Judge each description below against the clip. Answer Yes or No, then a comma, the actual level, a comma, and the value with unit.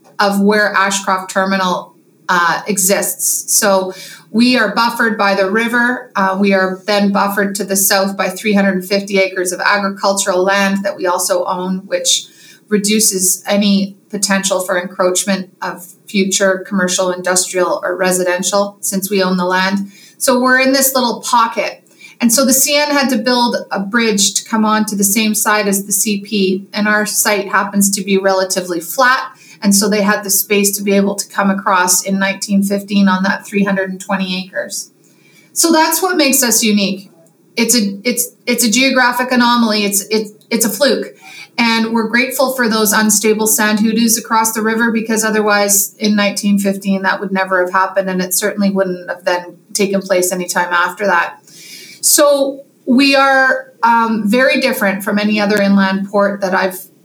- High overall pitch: Yes, high, 200 Hz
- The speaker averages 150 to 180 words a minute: Yes, average, 170 wpm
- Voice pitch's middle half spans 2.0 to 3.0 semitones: Yes, average, 2.7 semitones